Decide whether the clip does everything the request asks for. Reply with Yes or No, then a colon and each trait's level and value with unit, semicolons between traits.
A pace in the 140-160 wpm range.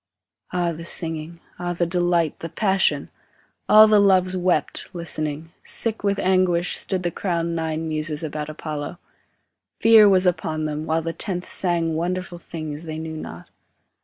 Yes: average, 155 wpm